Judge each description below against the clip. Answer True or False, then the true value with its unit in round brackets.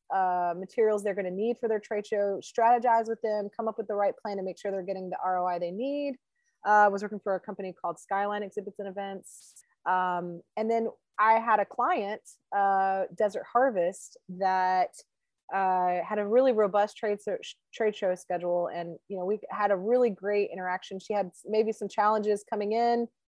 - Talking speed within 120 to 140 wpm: False (200 wpm)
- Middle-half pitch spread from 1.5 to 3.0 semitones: True (2.7 semitones)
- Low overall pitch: False (205 Hz)